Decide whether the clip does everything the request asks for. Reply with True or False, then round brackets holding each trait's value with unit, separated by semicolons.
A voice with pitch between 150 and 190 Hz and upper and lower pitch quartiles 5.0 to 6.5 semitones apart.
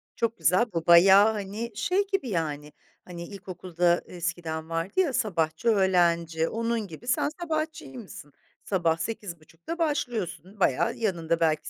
True (185 Hz; 5.5 semitones)